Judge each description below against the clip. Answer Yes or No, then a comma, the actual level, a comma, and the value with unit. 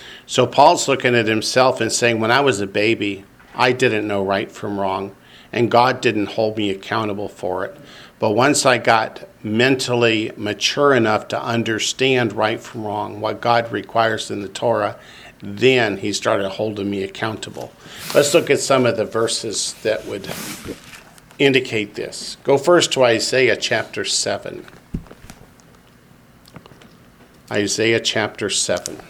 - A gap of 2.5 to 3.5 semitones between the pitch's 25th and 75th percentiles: Yes, average, 3.1 semitones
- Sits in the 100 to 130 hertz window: Yes, low, 115 Hz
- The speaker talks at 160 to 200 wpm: No, average, 145 wpm